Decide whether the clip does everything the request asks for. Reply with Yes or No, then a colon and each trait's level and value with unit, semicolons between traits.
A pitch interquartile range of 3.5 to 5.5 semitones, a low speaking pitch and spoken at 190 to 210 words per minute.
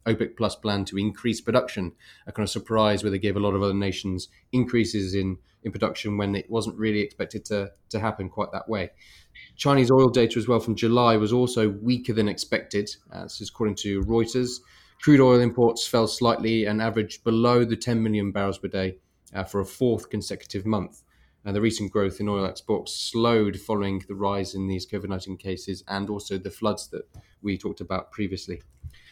No: narrow, 2.6 semitones; low, 105 Hz; average, 200 wpm